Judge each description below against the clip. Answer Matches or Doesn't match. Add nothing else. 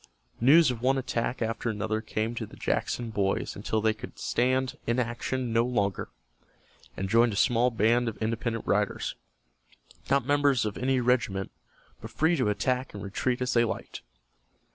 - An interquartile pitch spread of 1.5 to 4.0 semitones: Matches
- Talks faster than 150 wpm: Matches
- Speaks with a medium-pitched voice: Doesn't match